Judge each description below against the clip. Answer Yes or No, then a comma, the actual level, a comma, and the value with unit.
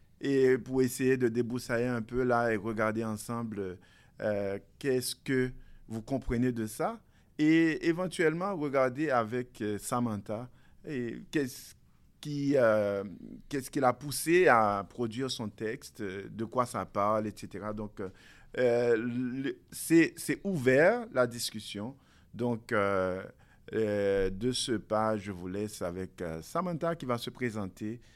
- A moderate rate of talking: No, slow, 130 wpm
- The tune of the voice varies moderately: Yes, average, 3.9 semitones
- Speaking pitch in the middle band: No, low, 120 Hz